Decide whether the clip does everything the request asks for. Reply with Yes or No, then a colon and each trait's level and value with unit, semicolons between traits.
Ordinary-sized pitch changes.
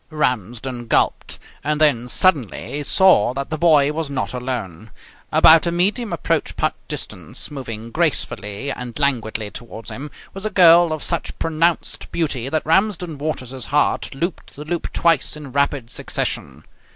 Yes: average, 4.9 semitones